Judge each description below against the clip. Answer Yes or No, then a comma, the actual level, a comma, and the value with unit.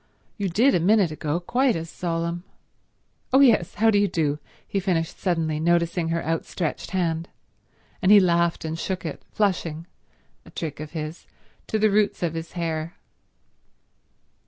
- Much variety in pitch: No, average, 3.2 semitones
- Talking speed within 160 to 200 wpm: No, average, 145 wpm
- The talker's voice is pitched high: No, medium, 170 Hz